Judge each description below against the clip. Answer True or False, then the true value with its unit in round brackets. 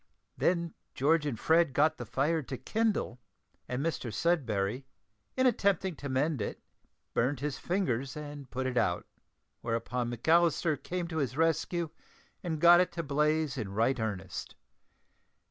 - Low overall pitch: False (145 Hz)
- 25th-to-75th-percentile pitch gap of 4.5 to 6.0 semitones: True (5.1 semitones)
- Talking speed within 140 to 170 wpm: True (145 wpm)